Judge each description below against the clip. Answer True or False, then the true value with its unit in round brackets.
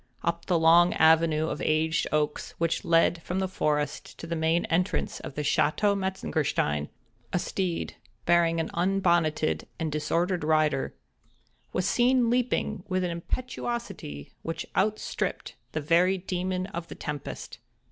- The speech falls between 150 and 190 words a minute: False (140 wpm)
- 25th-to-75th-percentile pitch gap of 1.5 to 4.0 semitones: True (3.0 semitones)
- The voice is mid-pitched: True (170 Hz)